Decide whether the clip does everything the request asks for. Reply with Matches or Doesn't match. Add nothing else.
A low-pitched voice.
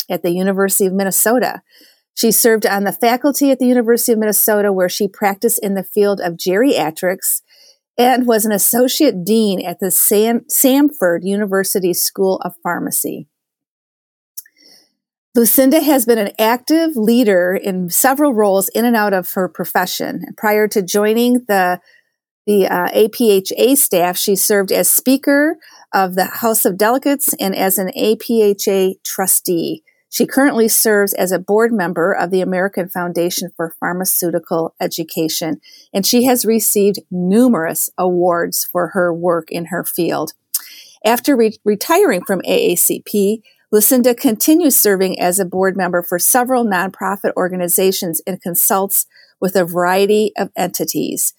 Doesn't match